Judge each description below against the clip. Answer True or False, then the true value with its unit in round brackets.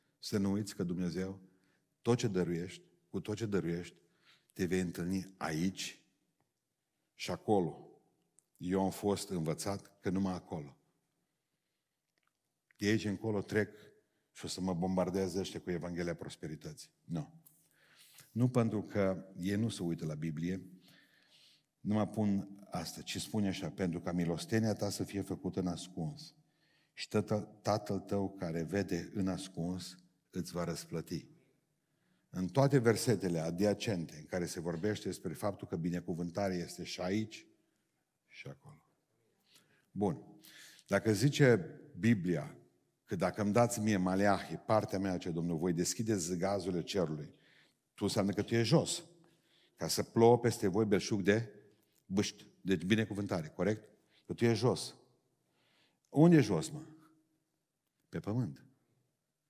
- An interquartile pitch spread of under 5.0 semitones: True (3.5 semitones)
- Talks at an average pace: True (140 wpm)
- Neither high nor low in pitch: False (100 Hz)